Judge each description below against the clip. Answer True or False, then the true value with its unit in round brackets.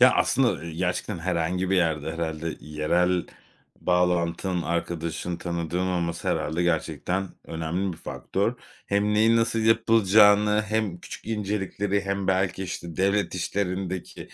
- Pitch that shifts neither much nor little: True (3.1 semitones)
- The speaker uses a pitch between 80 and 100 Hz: True (90 Hz)